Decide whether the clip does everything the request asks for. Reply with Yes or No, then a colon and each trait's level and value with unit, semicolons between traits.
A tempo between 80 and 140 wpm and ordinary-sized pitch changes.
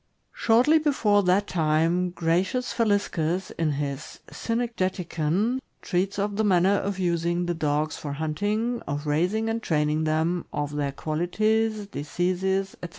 Yes: slow, 135 wpm; average, 4.8 semitones